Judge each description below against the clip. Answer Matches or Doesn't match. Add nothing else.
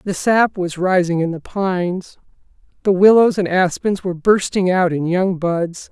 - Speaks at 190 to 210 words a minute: Doesn't match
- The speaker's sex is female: Matches